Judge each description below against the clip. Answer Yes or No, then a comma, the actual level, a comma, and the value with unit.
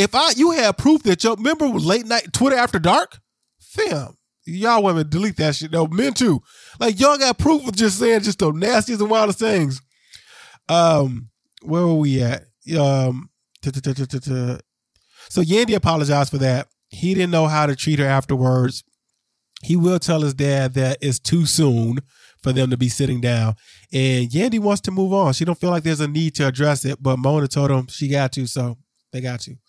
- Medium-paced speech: No, fast, 210 wpm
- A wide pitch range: Yes, wide, 6.7 semitones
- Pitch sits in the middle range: Yes, medium, 150 Hz